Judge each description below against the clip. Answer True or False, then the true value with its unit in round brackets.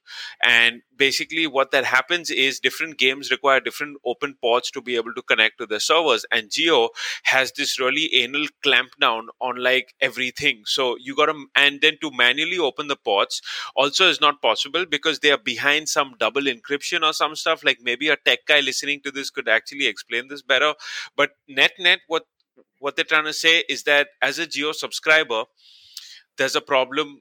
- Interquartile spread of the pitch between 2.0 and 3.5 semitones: True (2.7 semitones)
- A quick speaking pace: False (190 wpm)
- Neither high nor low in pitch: True (145 Hz)